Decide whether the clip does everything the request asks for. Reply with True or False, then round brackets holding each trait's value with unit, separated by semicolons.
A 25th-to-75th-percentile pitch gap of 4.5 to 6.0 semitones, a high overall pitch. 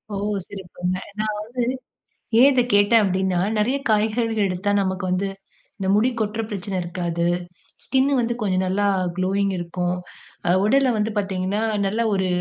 False (2.7 semitones; 200 Hz)